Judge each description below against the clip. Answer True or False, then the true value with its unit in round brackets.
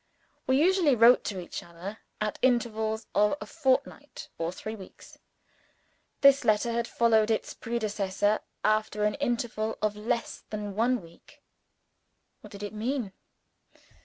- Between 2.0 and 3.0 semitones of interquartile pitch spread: True (2.7 semitones)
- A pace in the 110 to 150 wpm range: True (135 wpm)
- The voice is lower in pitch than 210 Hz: False (220 Hz)